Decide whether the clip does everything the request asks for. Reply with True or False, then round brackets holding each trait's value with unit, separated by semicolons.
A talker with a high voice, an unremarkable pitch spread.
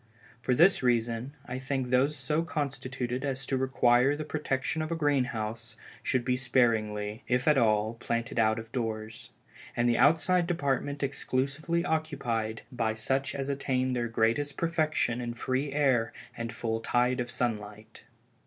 False (125 Hz; 3.4 semitones)